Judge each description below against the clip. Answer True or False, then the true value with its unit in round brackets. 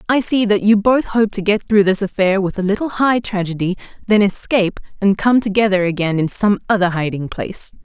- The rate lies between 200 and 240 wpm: True (205 wpm)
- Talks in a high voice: True (200 Hz)